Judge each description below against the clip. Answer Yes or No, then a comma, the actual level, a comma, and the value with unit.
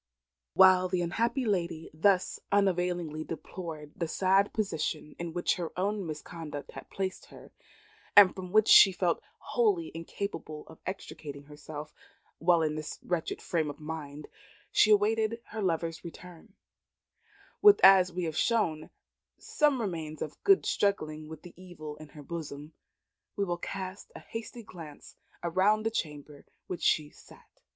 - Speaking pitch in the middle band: Yes, medium, 175 Hz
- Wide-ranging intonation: No, average, 4.2 semitones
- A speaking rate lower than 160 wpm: Yes, average, 150 wpm